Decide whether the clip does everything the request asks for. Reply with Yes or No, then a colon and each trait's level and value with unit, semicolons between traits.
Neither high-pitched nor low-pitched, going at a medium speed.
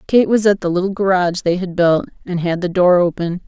No: medium, 180 Hz; fast, 240 wpm